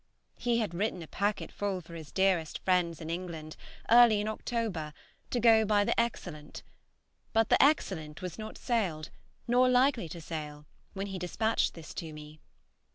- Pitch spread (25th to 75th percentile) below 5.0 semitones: No, wide, 5.6 semitones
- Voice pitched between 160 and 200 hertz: Yes, high, 190 Hz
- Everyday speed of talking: Yes, average, 165 wpm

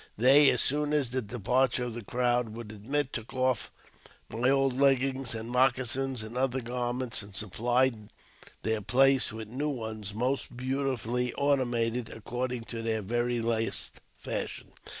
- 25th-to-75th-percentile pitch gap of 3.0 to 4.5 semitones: No, narrow, 2.6 semitones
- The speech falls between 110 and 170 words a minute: Yes, average, 150 wpm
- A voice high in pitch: No, low, 125 Hz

